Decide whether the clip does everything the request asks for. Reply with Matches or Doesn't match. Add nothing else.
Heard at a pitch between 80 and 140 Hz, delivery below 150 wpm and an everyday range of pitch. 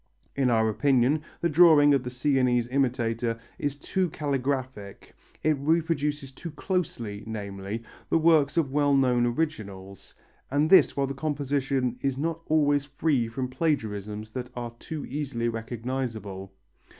Matches